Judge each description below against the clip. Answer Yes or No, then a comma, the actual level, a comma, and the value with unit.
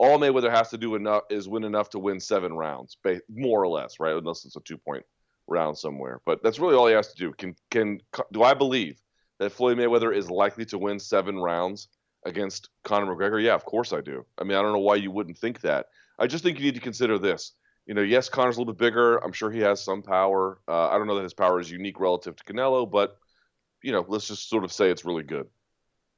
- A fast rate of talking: Yes, fast, 250 wpm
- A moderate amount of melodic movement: Yes, average, 3.5 semitones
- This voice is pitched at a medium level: No, low, 100 Hz